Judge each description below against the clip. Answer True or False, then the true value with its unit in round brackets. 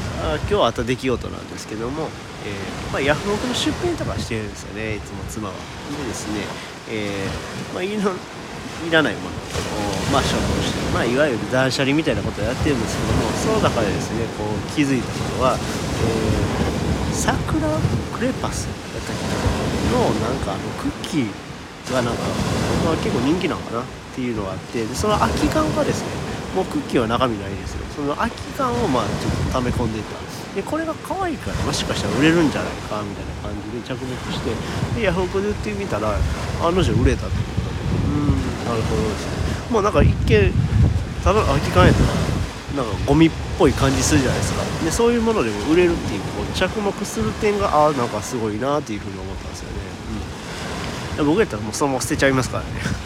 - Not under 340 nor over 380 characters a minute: False (425 characters per minute)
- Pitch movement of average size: False (6.1 semitones)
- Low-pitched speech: True (115 Hz)